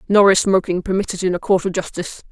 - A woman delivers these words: Yes, female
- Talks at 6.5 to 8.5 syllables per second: Yes, 6.7 syllables/s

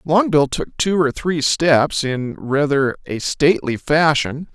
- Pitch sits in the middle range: Yes, medium, 150 Hz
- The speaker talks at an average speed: Yes, average, 145 wpm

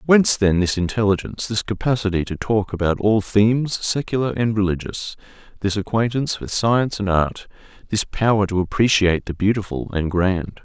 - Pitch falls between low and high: No, low, 105 Hz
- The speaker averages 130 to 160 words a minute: Yes, average, 140 wpm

